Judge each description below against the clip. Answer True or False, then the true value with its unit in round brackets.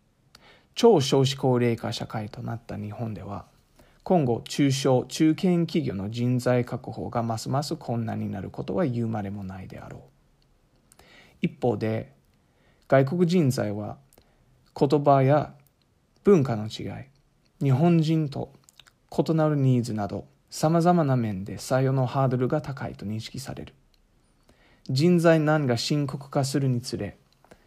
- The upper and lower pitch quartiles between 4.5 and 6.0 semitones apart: True (5.0 semitones)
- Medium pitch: False (130 Hz)